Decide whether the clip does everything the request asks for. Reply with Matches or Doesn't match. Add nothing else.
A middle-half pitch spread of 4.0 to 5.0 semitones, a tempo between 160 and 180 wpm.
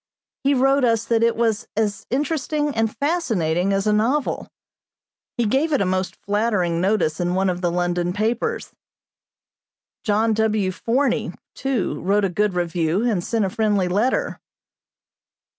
Doesn't match